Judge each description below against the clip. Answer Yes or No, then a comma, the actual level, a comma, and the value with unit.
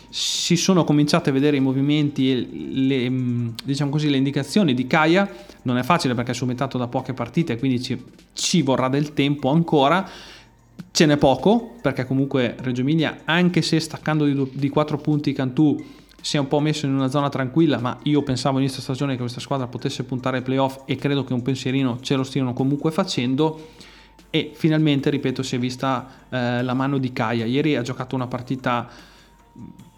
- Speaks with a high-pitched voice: No, low, 135 Hz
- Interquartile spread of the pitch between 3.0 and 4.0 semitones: No, narrow, 2.6 semitones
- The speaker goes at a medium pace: No, fast, 190 wpm